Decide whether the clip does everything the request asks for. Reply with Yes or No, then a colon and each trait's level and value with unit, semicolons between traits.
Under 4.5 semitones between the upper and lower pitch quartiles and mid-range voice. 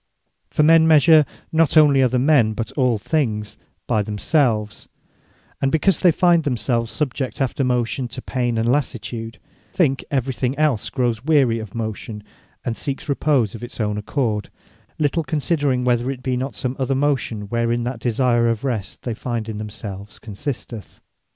No: average, 3.9 semitones; low, 125 Hz